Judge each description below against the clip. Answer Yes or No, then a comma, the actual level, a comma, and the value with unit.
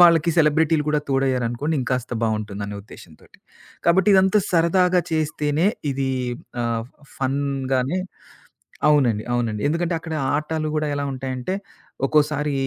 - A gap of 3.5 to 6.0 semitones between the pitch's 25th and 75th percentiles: Yes, average, 4.2 semitones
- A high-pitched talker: No, medium, 145 Hz